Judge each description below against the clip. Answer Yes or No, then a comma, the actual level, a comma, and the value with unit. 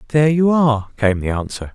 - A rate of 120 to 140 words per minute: No, fast, 205 wpm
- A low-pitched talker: Yes, low, 130 Hz